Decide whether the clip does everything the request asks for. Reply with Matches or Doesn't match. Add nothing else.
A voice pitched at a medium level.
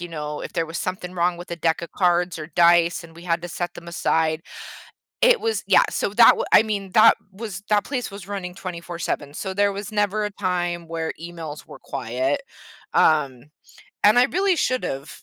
Matches